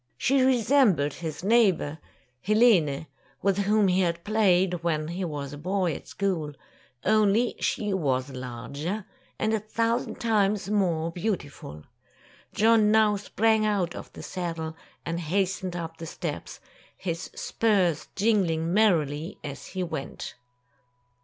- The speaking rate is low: Yes, slow, 130 wpm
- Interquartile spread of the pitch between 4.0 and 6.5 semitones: Yes, average, 4.8 semitones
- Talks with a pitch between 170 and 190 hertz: Yes, medium, 185 Hz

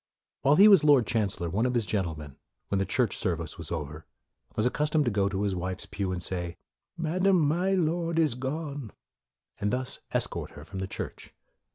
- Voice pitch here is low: Yes, low, 110 Hz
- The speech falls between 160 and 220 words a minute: Yes, average, 195 wpm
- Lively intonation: Yes, wide, 8.5 semitones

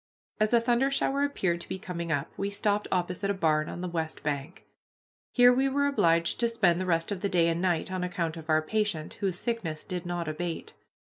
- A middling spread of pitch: Yes, average, 4.2 semitones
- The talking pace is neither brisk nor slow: No, fast, 220 wpm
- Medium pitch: Yes, medium, 180 Hz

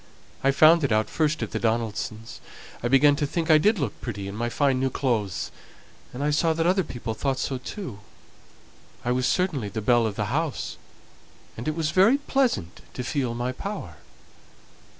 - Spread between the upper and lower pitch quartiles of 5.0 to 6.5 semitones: Yes, wide, 5.4 semitones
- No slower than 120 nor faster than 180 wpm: No, average, 190 wpm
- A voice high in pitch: No, low, 135 Hz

